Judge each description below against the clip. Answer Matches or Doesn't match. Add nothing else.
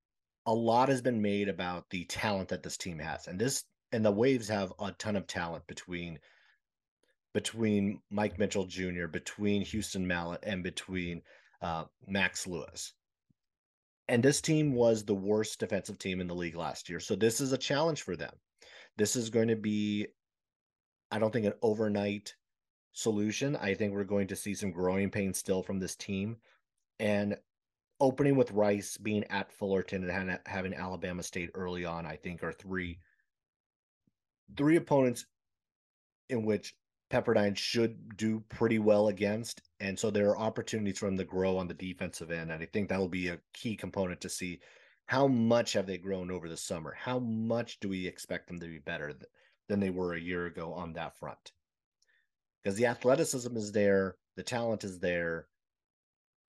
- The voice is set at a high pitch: Doesn't match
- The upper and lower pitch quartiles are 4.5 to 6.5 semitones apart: Doesn't match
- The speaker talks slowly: Doesn't match